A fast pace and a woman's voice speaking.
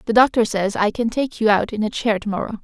Yes: fast, 295 wpm; female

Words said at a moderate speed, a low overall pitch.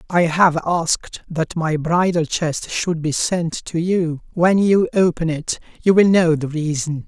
No: average, 180 wpm; medium, 165 Hz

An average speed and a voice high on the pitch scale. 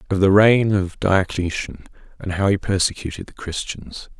No: average, 155 wpm; very low, 95 Hz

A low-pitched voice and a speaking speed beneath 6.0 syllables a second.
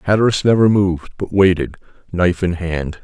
Yes: very low, 90 Hz; 5.7 syllables/s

